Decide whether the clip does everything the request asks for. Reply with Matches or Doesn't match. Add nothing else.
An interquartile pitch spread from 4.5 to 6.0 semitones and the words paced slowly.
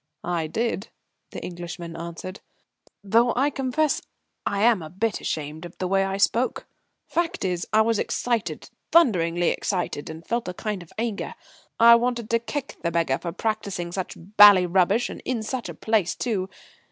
Doesn't match